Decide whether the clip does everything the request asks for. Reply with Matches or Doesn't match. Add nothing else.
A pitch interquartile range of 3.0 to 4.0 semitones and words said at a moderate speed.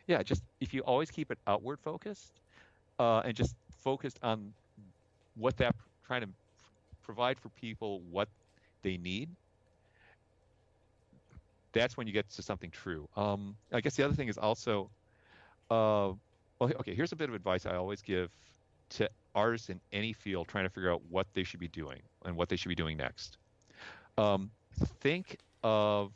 Matches